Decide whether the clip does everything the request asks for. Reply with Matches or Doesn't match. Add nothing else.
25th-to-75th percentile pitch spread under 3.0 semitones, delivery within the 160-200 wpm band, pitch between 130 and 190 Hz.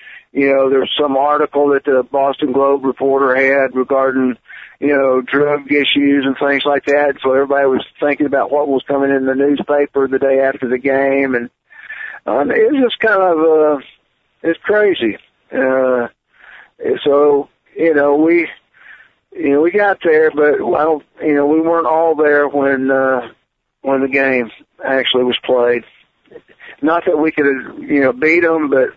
Matches